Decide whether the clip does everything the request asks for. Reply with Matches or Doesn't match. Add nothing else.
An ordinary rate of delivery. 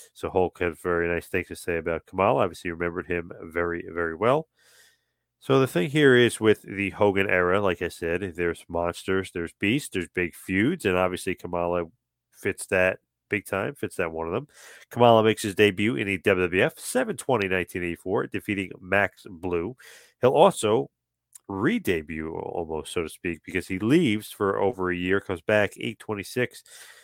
Matches